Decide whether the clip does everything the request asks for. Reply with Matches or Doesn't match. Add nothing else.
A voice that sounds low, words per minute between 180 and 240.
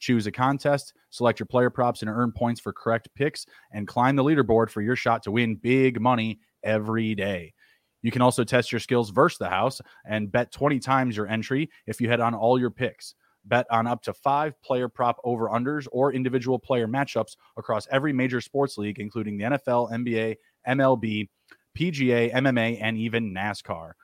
Matches